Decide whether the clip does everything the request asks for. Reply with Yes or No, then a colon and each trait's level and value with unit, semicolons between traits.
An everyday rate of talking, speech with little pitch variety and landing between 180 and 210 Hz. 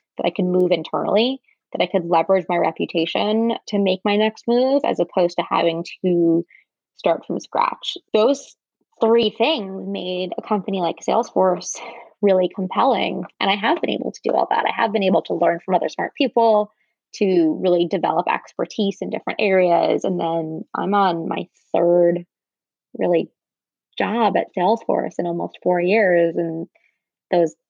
No: average, 165 wpm; average, 3.8 semitones; high, 190 Hz